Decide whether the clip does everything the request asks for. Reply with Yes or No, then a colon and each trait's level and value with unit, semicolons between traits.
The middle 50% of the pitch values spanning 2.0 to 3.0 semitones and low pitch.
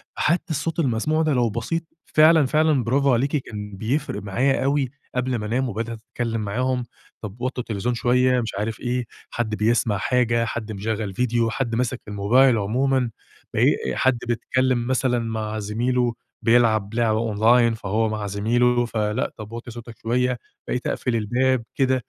Yes: average, 2.7 semitones; low, 120 Hz